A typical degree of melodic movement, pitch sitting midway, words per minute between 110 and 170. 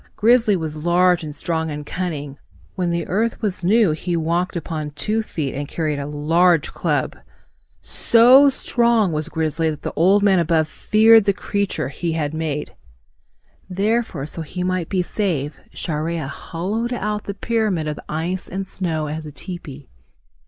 Yes: average, 4.6 semitones; medium, 170 Hz; average, 160 wpm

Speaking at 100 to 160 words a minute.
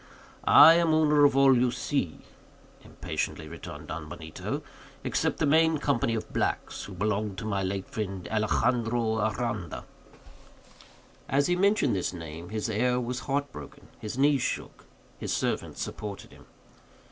Yes: average, 145 wpm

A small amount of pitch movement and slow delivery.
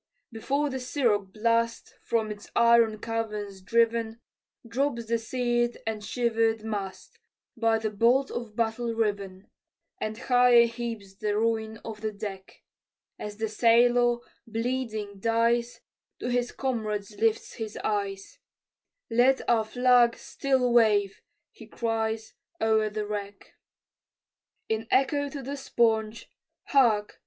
Yes: narrow, 2.0 semitones; slow, 125 wpm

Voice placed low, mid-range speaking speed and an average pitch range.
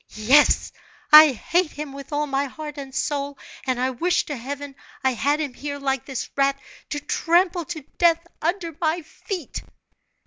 No: very high, 290 Hz; average, 170 wpm; average, 3.0 semitones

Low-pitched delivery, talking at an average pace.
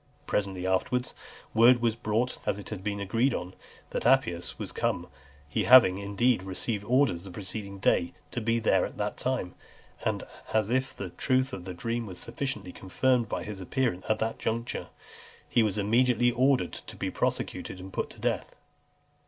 Yes: low, 110 Hz; average, 175 wpm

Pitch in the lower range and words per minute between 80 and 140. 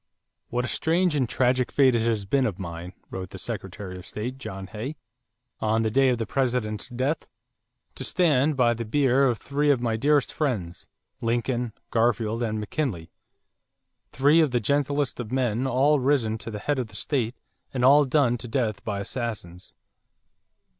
No: low, 120 Hz; average, 175 wpm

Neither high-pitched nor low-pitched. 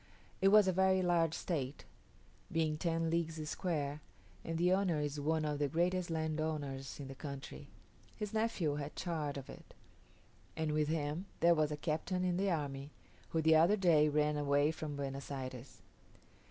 Yes: medium, 155 Hz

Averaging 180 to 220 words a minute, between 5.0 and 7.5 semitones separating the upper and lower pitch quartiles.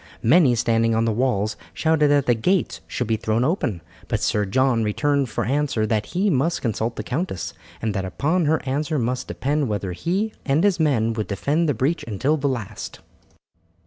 Yes: average, 190 wpm; wide, 5.5 semitones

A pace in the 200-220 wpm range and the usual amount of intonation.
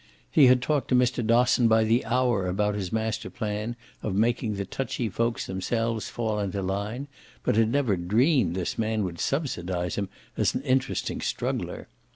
No: average, 175 wpm; average, 3.7 semitones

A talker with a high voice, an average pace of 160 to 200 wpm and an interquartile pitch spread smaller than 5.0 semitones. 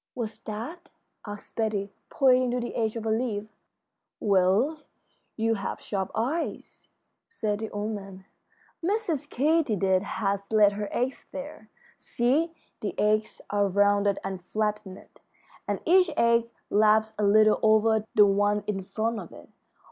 No: high, 215 Hz; average, 140 wpm; average, 2.7 semitones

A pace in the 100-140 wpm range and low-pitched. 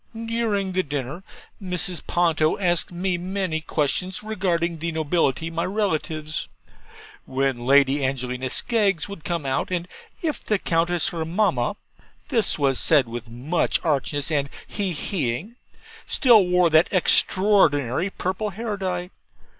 No: slow, 135 wpm; medium, 170 Hz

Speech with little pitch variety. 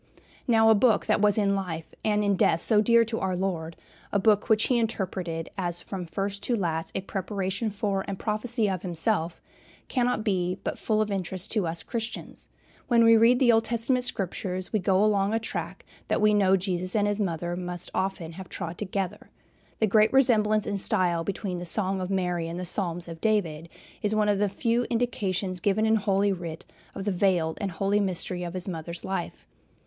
No: average, 3.2 semitones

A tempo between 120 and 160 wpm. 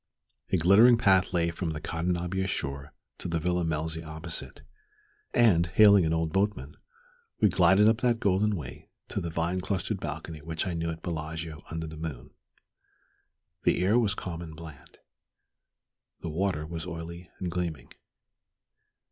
Yes: average, 155 wpm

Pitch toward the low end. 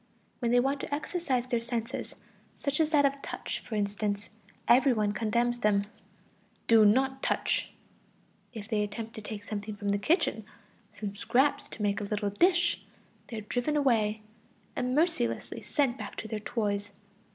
No: high, 230 Hz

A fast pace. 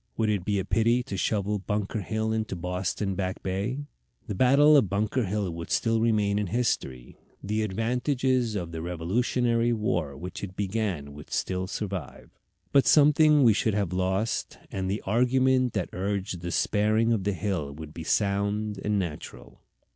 No: average, 170 wpm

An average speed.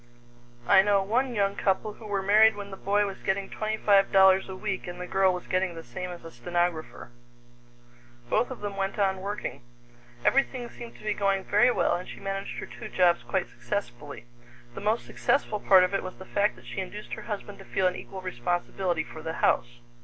No: fast, 215 wpm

